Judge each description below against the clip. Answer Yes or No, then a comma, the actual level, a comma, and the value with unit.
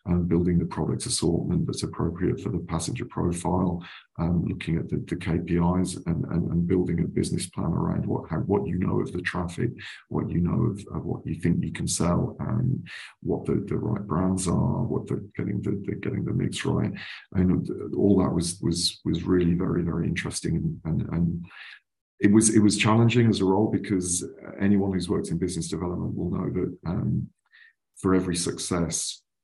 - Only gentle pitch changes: Yes, narrow, 1.7 semitones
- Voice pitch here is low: Yes, very low, 90 Hz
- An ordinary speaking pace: Yes, average, 190 wpm